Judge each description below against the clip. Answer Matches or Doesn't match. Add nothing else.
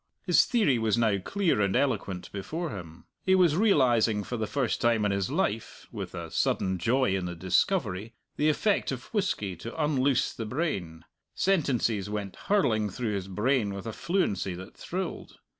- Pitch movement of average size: Doesn't match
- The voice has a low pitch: Matches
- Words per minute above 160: Matches